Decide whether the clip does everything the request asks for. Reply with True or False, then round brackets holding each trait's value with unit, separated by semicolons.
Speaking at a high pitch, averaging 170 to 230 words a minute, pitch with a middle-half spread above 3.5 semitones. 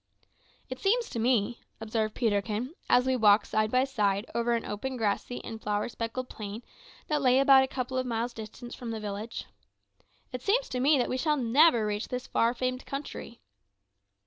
False (240 Hz; 185 wpm; 3.0 semitones)